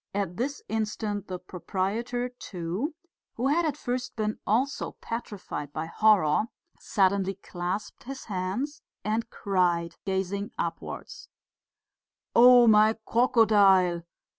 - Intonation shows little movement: No, average, 4.5 semitones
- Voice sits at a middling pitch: No, high, 210 Hz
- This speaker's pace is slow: Yes, slow, 110 wpm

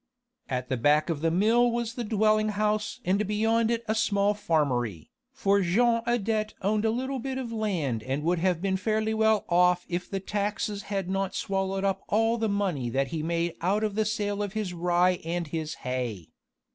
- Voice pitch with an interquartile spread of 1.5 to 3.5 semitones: No, average, 4.2 semitones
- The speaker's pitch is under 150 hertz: No, high, 200 Hz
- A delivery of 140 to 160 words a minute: No, average, 195 wpm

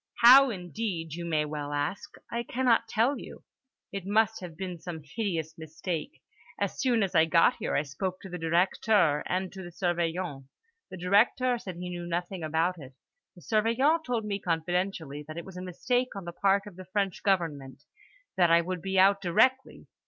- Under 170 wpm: No, average, 190 wpm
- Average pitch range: Yes, average, 3.8 semitones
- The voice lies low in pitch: No, medium, 180 Hz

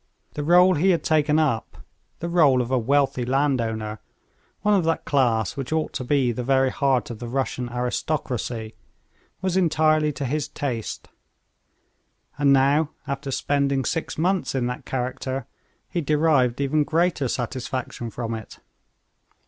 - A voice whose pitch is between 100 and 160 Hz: Yes, low, 135 Hz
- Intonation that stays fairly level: No, average, 3.7 semitones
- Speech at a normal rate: Yes, average, 150 wpm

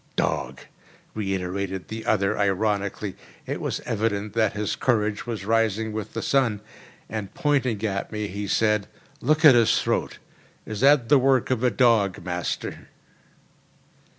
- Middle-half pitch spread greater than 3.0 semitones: No, average, 2.7 semitones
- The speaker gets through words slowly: No, average, 145 wpm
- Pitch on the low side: Yes, low, 110 Hz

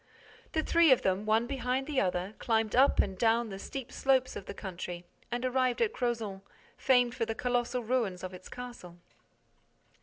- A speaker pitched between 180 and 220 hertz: No, high, 240 Hz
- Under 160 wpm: No, average, 180 wpm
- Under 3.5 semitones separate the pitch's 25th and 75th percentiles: No, average, 4.6 semitones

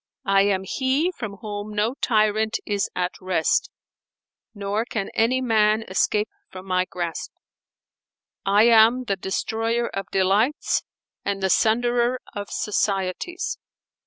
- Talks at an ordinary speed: No, slow, 125 wpm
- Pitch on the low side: No, high, 210 Hz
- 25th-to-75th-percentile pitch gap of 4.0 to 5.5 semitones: No, average, 3.2 semitones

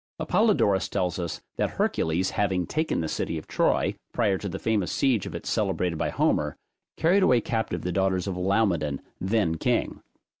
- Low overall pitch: Yes, very low, 95 Hz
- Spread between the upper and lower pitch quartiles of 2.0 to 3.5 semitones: No, average, 4.1 semitones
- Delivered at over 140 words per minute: Yes, average, 175 wpm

